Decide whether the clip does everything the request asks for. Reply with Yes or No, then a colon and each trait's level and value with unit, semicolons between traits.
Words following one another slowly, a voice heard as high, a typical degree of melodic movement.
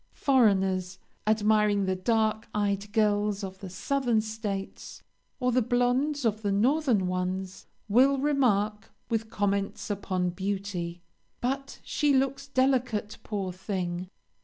Yes: slow, 120 wpm; high, 210 Hz; average, 4.3 semitones